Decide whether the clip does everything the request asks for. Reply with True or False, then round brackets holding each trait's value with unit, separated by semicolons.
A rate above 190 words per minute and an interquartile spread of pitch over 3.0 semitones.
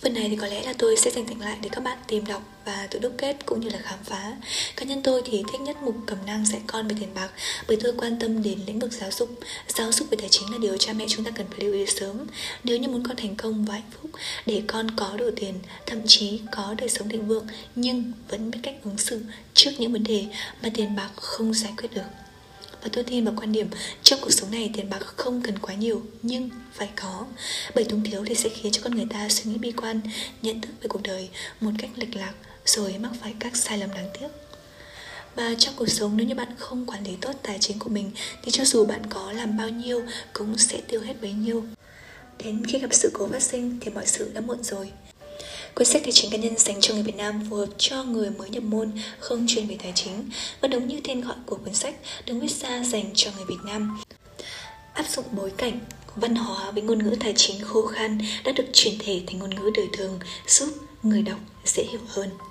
False (250 wpm; 2.7 semitones)